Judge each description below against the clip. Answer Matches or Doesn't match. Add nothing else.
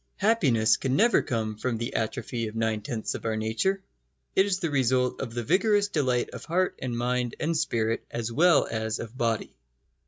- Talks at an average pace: Matches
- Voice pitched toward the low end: Matches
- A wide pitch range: Matches